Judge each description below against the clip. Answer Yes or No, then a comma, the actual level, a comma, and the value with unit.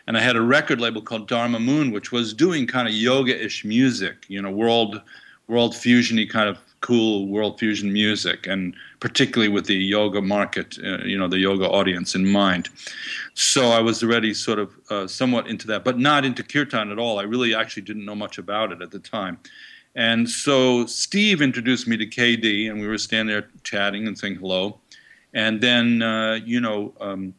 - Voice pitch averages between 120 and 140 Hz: No, low, 110 Hz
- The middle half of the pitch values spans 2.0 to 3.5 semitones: Yes, average, 2.7 semitones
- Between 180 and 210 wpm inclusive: Yes, average, 200 wpm